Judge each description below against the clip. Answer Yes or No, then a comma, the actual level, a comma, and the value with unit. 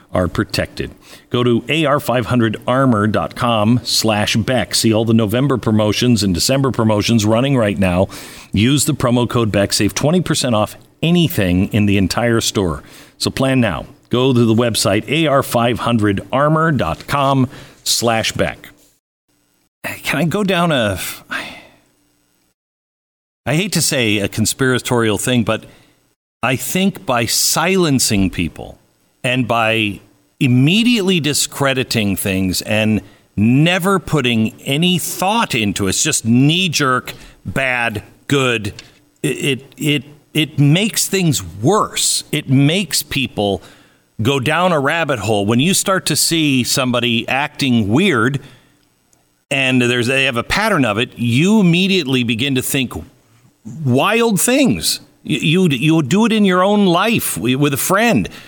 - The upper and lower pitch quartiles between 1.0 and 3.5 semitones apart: No, average, 5.3 semitones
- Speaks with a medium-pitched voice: No, low, 125 Hz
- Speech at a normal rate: No, slow, 130 wpm